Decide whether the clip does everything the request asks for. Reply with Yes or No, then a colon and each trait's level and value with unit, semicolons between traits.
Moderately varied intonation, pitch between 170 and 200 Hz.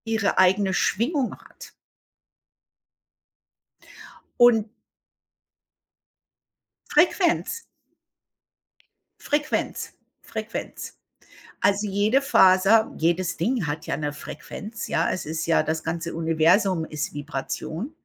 No: wide, 5.7 semitones; high, 190 Hz